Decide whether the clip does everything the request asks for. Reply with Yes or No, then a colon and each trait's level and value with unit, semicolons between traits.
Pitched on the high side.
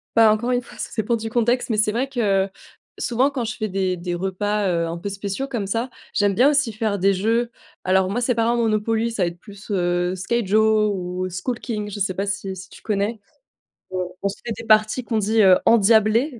Yes: high, 215 Hz